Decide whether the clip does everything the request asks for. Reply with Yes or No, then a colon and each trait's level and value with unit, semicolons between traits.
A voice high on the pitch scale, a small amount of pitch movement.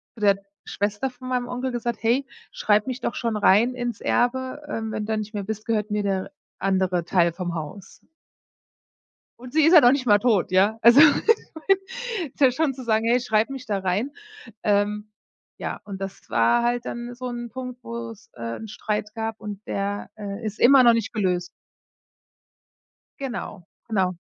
No: high, 225 Hz; average, 3.7 semitones